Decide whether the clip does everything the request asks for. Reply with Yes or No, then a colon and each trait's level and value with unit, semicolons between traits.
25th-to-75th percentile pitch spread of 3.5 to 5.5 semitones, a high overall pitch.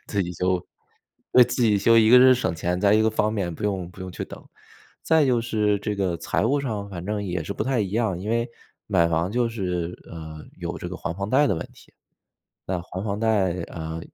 No: average, 4.0 semitones; low, 100 Hz